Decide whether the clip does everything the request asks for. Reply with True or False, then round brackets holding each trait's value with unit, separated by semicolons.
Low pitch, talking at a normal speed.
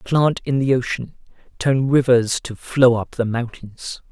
True (125 Hz; 160 wpm)